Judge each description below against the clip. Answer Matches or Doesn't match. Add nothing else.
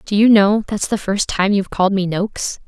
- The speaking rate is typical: Doesn't match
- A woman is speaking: Matches